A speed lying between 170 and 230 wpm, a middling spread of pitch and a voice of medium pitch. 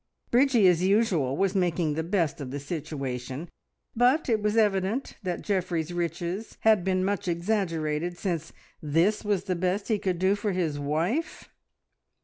No: average, 155 wpm; average, 4.1 semitones; medium, 180 Hz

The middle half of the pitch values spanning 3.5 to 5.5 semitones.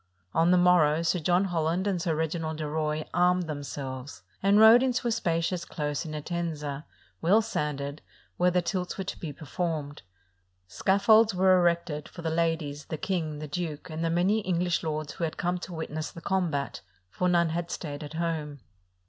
No: average, 2.9 semitones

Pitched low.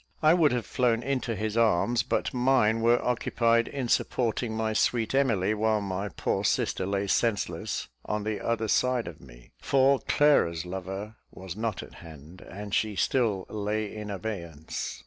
Yes: low, 110 Hz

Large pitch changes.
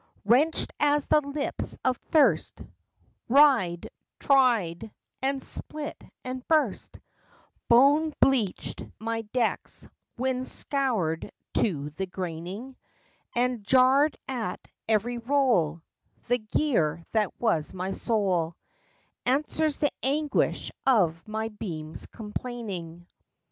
Yes: wide, 6.4 semitones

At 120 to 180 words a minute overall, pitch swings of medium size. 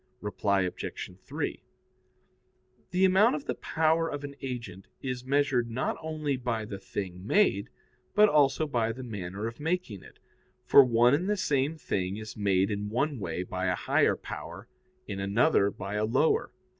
No: average, 170 wpm; wide, 6.8 semitones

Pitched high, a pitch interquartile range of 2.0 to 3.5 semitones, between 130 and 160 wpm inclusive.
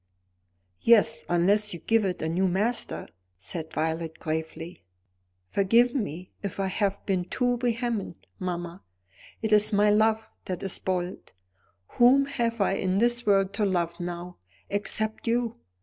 No: high, 200 Hz; average, 4.3 semitones; average, 145 wpm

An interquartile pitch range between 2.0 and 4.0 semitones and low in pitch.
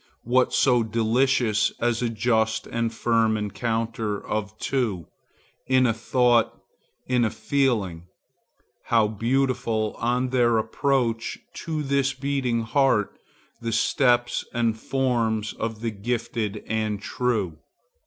Yes: narrow, 2.4 semitones; low, 115 Hz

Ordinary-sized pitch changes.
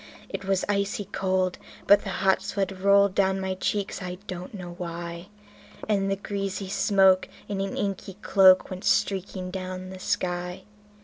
No: narrow, 1.2 semitones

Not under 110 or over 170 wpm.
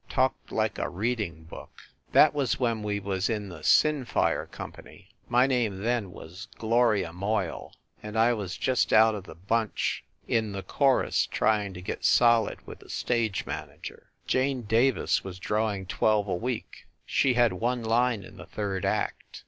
Yes: average, 165 wpm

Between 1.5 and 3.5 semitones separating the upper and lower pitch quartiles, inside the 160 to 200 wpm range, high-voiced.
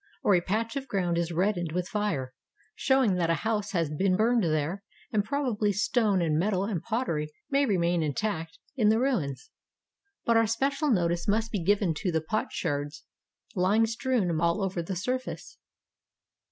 No: average, 5.0 semitones; average, 175 wpm; high, 195 Hz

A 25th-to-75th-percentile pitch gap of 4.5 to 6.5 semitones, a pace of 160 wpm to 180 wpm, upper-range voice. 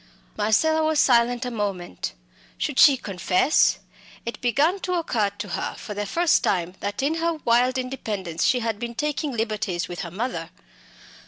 Yes: wide, 5.5 semitones; average, 165 wpm; high, 235 Hz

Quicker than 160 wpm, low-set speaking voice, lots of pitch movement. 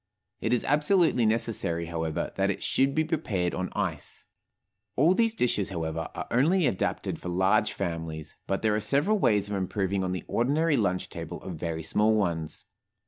Yes: average, 175 wpm; low, 100 Hz; wide, 7.9 semitones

